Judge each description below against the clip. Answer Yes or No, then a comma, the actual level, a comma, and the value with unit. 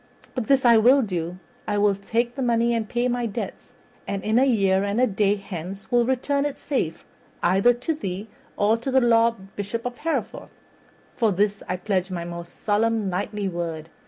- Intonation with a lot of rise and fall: No, average, 3.9 semitones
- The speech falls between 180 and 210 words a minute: Yes, average, 190 wpm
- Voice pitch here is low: No, high, 215 Hz